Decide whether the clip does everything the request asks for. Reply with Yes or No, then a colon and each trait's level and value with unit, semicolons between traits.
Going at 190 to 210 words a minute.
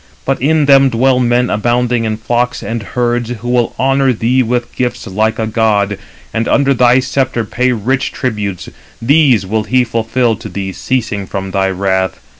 No: average, 175 wpm